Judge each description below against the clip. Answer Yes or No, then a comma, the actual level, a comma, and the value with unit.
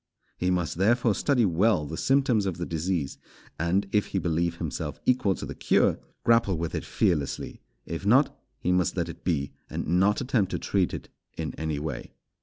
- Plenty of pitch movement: No, average, 4.1 semitones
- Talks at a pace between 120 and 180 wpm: No, average, 190 wpm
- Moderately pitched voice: No, very low, 90 Hz